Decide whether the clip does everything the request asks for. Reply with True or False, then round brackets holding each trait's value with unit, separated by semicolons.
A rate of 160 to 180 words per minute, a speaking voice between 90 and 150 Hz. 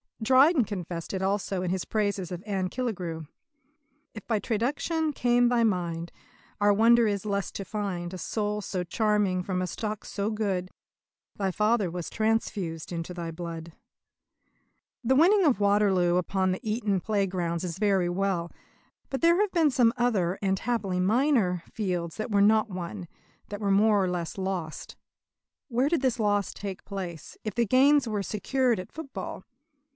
False (165 wpm; 200 Hz)